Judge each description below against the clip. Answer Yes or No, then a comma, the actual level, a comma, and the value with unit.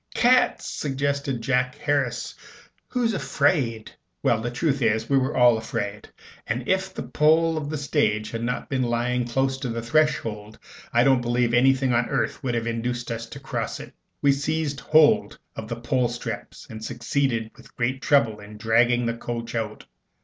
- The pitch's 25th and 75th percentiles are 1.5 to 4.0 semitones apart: Yes, average, 3.3 semitones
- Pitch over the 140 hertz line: No, low, 125 Hz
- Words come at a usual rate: Yes, average, 175 wpm